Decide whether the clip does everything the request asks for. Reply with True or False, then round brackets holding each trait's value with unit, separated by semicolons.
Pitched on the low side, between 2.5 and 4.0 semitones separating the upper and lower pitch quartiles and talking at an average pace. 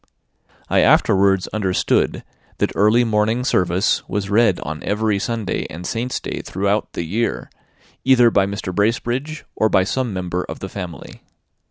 True (105 Hz; 3.4 semitones; 150 wpm)